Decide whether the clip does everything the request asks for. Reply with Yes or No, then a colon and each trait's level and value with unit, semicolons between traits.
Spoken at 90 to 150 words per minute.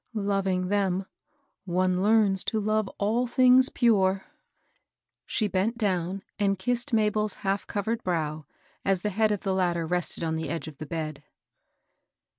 Yes: average, 145 wpm